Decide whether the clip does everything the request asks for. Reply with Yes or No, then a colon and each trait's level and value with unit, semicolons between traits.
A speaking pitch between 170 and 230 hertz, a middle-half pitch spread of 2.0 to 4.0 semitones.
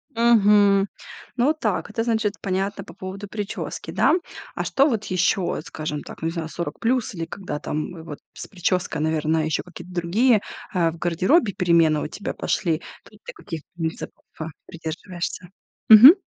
No: medium, 185 Hz; average, 4.4 semitones